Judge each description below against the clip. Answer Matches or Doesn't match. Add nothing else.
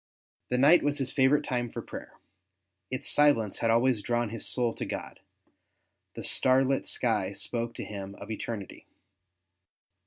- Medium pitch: Doesn't match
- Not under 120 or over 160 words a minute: Matches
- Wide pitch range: Doesn't match